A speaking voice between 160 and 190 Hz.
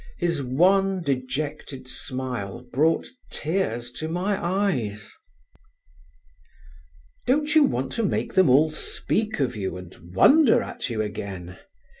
No: medium, 140 Hz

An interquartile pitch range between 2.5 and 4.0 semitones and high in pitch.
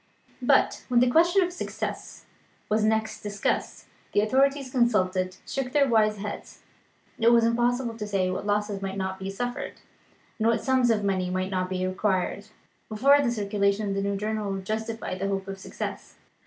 Yes: average, 3.5 semitones; high, 210 Hz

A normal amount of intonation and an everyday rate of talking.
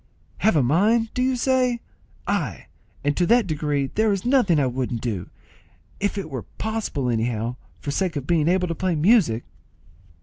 No: wide, 8.4 semitones; average, 180 wpm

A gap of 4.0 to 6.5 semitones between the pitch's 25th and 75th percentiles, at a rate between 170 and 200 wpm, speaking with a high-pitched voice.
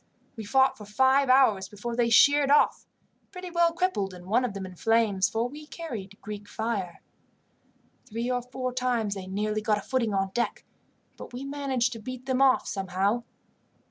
Yes: average, 4.4 semitones; average, 180 wpm; high, 235 Hz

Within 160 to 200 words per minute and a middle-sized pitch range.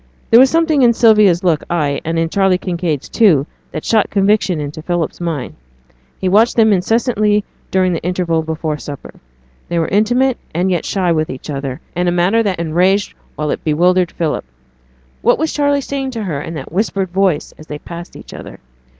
Yes: average, 190 wpm; average, 4.7 semitones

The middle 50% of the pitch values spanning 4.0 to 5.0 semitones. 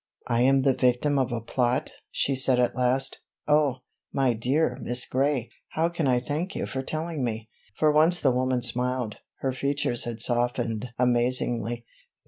No: narrow, 2.5 semitones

